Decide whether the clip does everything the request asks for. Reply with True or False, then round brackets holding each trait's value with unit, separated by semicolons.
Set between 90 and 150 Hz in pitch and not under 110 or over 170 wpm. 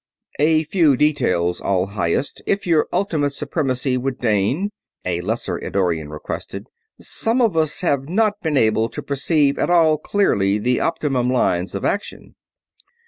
True (140 Hz; 145 wpm)